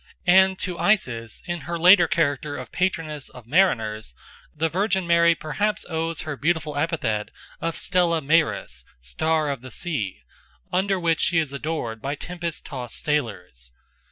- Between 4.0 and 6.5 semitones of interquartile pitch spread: Yes, average, 4.9 semitones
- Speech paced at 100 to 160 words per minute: Yes, average, 150 wpm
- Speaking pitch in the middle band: Yes, medium, 160 Hz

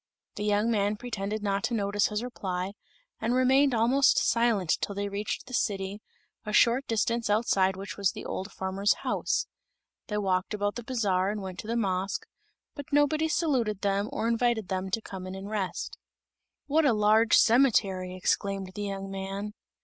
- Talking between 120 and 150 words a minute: No, average, 175 wpm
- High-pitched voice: Yes, high, 210 Hz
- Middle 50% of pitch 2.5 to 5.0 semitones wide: Yes, average, 3.1 semitones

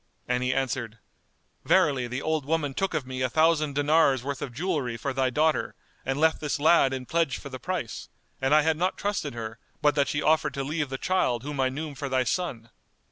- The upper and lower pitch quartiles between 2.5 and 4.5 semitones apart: Yes, average, 3.4 semitones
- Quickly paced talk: Yes, fast, 220 wpm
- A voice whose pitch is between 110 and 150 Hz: Yes, medium, 140 Hz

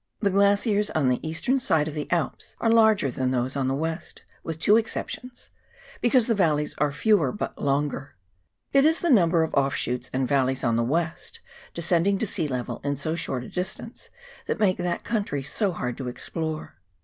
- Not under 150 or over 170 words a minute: No, average, 195 wpm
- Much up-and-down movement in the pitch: Yes, wide, 6.8 semitones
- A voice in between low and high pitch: Yes, medium, 160 Hz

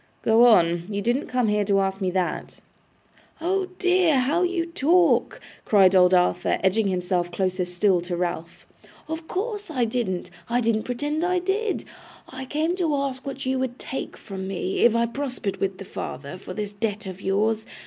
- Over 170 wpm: Yes, average, 180 wpm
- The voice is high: Yes, high, 225 Hz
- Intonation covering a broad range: Yes, wide, 7.3 semitones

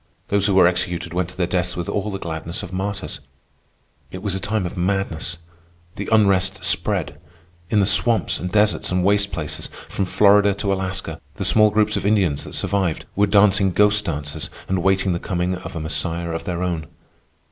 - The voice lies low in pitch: Yes, very low, 95 Hz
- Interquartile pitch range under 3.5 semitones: Yes, narrow, 2.6 semitones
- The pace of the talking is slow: No, average, 190 wpm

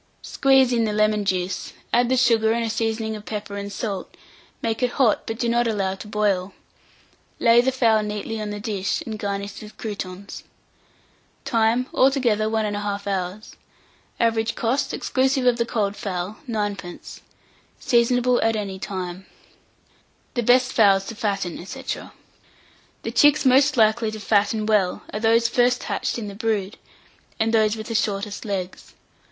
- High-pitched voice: Yes, high, 220 Hz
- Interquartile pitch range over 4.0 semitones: No, narrow, 2.6 semitones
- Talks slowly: No, average, 160 wpm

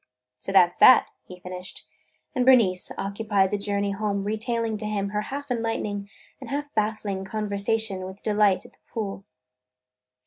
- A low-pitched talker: No, high, 205 Hz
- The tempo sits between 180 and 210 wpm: No, average, 160 wpm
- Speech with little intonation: Yes, narrow, 2.2 semitones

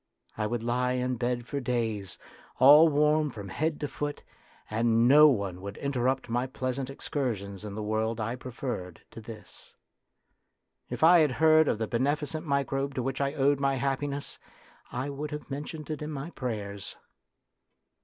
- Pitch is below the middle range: Yes, low, 130 Hz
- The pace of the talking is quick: No, average, 165 wpm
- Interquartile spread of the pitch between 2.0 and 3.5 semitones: No, average, 4.0 semitones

